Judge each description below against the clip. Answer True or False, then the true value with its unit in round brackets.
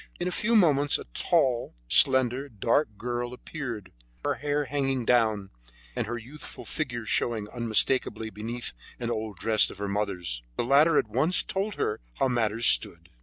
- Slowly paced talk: False (165 wpm)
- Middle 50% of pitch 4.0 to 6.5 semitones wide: True (4.5 semitones)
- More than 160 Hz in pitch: False (120 Hz)